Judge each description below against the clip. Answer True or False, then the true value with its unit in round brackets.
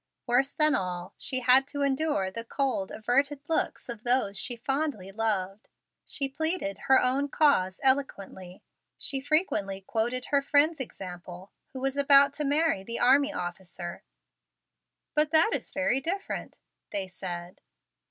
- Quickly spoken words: False (140 wpm)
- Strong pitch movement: True (6.5 semitones)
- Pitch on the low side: False (260 Hz)